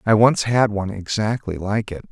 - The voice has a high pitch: No, low, 105 Hz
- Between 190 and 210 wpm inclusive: Yes, average, 200 wpm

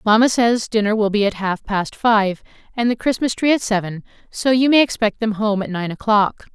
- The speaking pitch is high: Yes, high, 215 Hz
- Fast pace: Yes, fast, 220 wpm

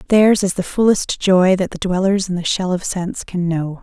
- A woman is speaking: Yes, female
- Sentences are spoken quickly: Yes, fast, 235 wpm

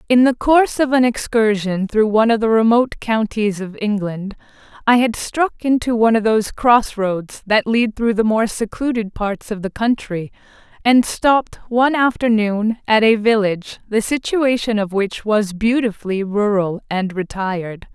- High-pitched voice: Yes, high, 220 Hz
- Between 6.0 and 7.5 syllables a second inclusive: No, 4.7 syllables/s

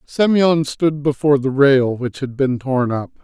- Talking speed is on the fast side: No, average, 185 wpm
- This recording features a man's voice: Yes, male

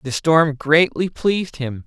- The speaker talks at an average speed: Yes, average, 160 wpm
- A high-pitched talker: No, medium, 150 Hz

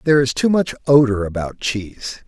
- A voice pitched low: Yes, low, 125 Hz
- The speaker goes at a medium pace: Yes, average, 185 wpm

